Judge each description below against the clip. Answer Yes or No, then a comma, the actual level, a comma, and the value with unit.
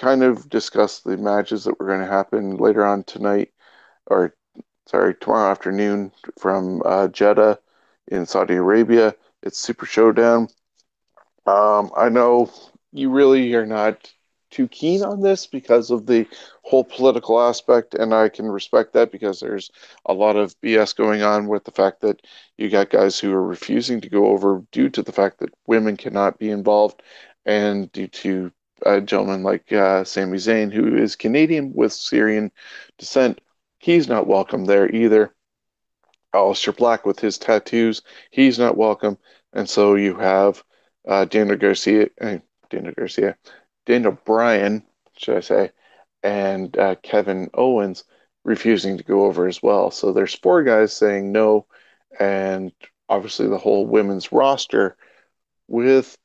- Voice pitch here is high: No, low, 105 Hz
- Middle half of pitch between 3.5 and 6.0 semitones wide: No, average, 2.9 semitones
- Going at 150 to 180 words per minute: Yes, average, 155 wpm